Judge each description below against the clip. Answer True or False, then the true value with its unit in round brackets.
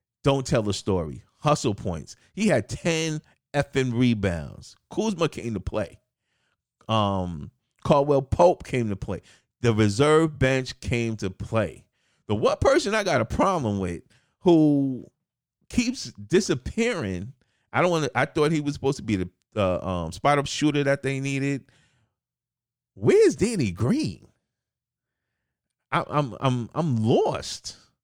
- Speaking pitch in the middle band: False (125 Hz)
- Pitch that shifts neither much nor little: False (6.0 semitones)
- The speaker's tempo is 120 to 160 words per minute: True (140 wpm)